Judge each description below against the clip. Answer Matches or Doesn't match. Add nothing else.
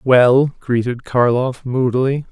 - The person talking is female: Doesn't match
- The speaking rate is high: Doesn't match